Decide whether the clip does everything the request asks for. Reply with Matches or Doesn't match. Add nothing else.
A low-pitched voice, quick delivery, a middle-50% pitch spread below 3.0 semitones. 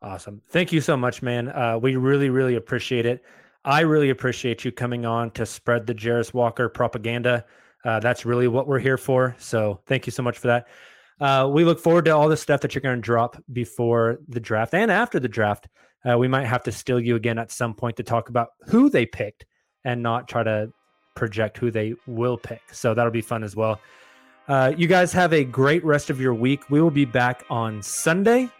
Matches